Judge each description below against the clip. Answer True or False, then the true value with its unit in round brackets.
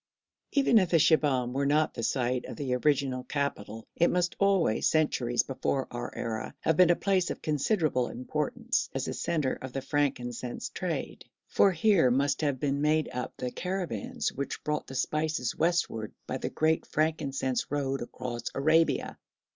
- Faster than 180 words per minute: False (165 wpm)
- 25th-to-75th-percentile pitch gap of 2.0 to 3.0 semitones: False (4.1 semitones)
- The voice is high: False (140 Hz)